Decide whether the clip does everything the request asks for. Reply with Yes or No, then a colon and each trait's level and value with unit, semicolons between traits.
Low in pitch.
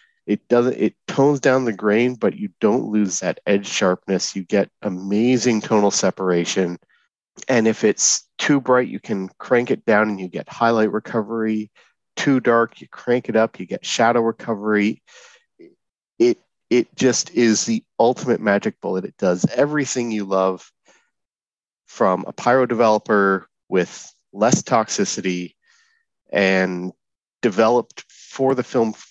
Yes: low, 115 Hz